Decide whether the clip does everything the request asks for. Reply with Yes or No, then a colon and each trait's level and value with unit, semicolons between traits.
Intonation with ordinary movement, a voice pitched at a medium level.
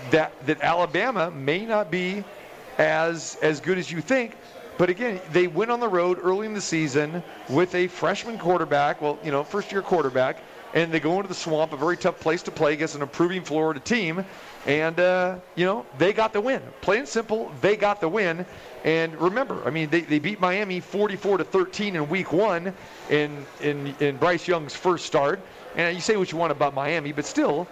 Yes: average, 3.3 semitones; medium, 175 Hz